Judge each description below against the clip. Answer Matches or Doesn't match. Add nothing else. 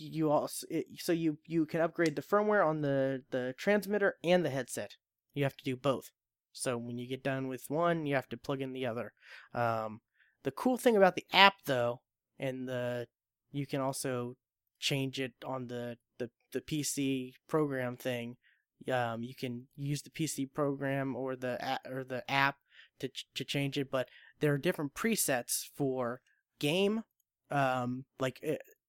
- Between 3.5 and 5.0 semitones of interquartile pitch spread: Doesn't match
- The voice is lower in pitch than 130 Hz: Doesn't match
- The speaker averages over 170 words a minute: Matches